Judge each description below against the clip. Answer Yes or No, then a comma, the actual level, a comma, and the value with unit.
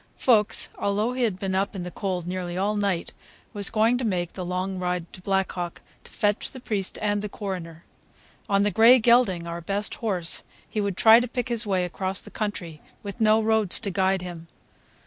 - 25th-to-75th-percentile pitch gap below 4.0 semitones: Yes, average, 3.0 semitones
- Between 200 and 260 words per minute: Yes, fast, 205 wpm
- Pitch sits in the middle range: No, high, 195 Hz